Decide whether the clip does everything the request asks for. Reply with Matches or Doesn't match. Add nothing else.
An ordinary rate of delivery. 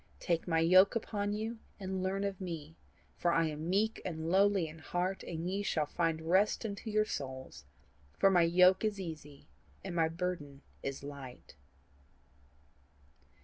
Matches